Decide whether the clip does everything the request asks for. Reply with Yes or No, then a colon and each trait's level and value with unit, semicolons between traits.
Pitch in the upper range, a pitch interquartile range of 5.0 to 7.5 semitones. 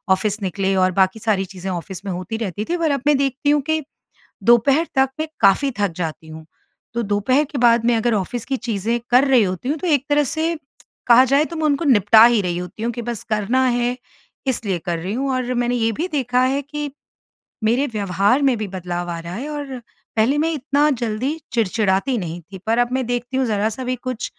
Yes: high, 240 Hz; wide, 5.4 semitones